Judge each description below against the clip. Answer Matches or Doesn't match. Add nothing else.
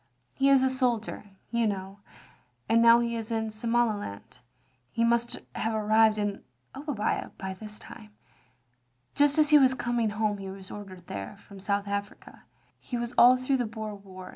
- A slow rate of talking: Doesn't match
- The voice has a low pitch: Doesn't match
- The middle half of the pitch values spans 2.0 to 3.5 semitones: Matches